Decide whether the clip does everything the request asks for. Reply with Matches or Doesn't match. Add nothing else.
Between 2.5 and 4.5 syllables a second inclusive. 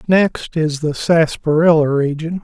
Matches